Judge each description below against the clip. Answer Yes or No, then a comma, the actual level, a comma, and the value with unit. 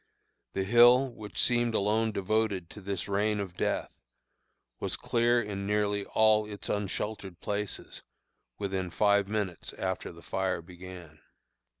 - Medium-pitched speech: No, low, 100 Hz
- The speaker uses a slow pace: Yes, slow, 130 wpm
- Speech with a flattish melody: Yes, narrow, 2.2 semitones